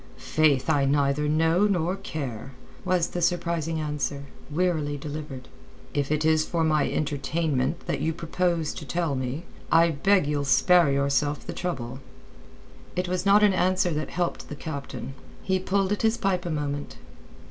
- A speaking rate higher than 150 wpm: Yes, average, 160 wpm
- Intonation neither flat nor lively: Yes, average, 3.7 semitones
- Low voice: No, medium, 155 Hz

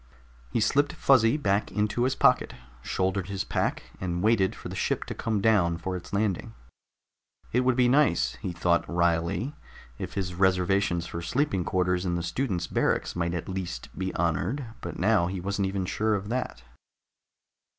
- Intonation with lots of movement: No, average, 4.3 semitones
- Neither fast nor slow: Yes, average, 170 wpm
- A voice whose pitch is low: Yes, very low, 95 Hz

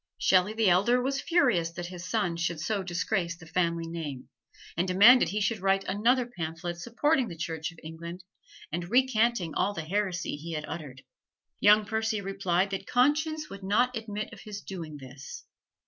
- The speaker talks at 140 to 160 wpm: No, average, 175 wpm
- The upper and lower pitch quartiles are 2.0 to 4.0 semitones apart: No, average, 4.6 semitones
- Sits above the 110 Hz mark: Yes, high, 190 Hz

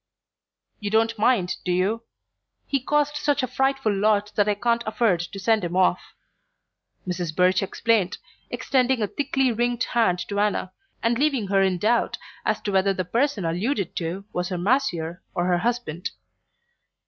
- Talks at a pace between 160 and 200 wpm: Yes, average, 165 wpm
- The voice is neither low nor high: No, high, 210 Hz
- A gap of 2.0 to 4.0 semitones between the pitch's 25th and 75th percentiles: No, average, 4.8 semitones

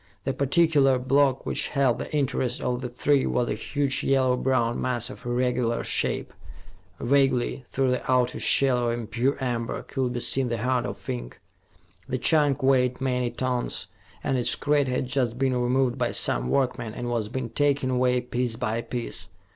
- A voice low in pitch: Yes, low, 125 Hz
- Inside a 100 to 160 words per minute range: No, average, 175 wpm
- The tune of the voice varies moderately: No, narrow, 1.8 semitones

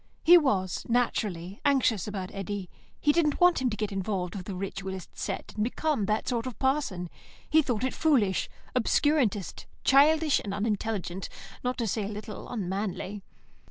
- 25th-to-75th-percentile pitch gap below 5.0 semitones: No, average, 5.3 semitones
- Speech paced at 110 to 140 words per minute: No, average, 160 wpm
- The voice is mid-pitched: No, high, 215 Hz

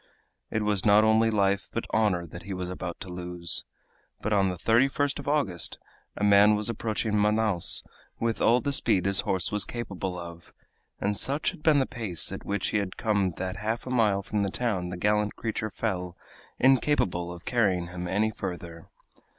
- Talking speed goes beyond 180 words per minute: Yes, average, 190 wpm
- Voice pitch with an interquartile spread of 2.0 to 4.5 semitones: Yes, average, 3.6 semitones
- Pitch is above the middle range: No, low, 105 Hz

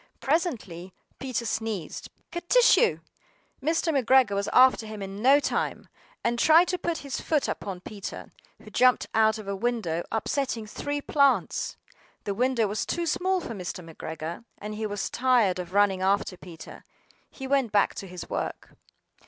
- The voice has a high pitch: Yes, high, 225 Hz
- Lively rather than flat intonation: Yes, wide, 5.9 semitones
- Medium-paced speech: Yes, average, 160 wpm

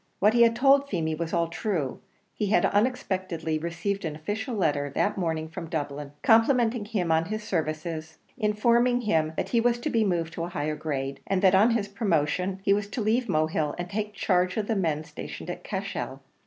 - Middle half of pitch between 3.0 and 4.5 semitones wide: No, average, 5.3 semitones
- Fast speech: Yes, fast, 210 wpm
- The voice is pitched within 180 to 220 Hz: Yes, medium, 185 Hz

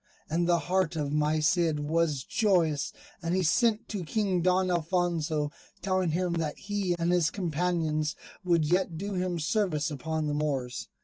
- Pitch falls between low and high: Yes, medium, 170 Hz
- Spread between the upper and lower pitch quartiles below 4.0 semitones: Yes, average, 3.0 semitones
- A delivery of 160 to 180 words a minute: Yes, average, 165 wpm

